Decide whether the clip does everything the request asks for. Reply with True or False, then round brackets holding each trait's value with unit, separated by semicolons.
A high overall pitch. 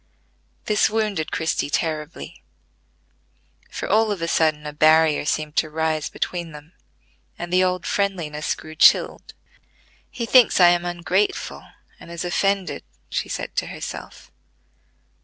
False (170 Hz)